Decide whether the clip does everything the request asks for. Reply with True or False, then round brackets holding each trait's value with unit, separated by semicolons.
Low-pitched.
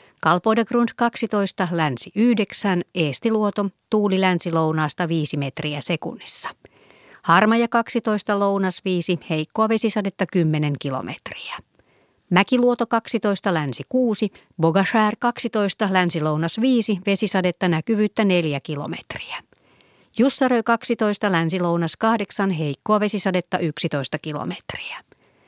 False (195 Hz)